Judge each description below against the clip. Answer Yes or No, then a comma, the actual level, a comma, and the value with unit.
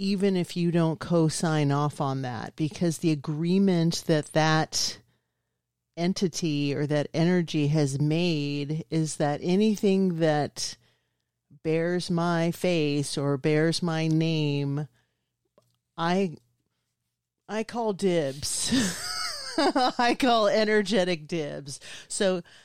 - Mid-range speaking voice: Yes, medium, 160 Hz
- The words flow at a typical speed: No, slow, 105 wpm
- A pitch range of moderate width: Yes, average, 3.7 semitones